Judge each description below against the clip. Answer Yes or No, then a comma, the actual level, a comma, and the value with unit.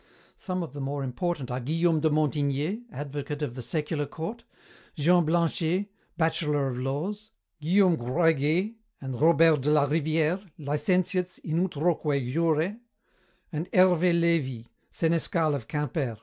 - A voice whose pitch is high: No, medium, 155 Hz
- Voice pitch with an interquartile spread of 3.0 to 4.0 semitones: Yes, average, 3.4 semitones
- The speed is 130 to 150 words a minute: Yes, slow, 135 wpm